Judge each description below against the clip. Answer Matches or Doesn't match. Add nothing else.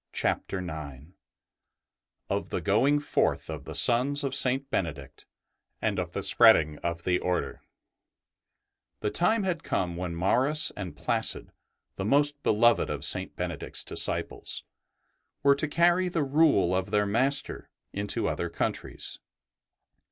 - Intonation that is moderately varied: Doesn't match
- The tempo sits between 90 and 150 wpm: Matches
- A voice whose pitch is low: Matches